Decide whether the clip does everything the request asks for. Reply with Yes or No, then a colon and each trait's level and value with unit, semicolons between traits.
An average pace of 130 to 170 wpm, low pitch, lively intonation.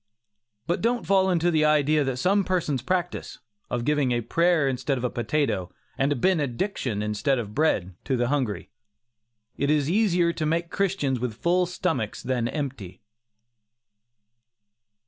No: average, 150 wpm; medium, 145 Hz; wide, 6.0 semitones